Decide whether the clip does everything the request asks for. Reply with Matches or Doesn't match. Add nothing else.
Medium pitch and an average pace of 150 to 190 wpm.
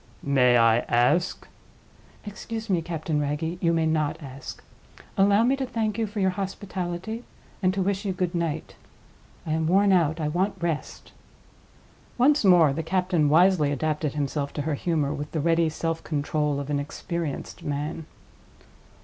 Matches